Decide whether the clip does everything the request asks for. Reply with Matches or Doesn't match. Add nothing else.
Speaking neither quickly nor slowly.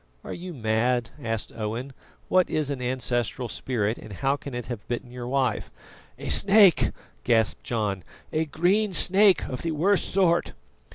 Matches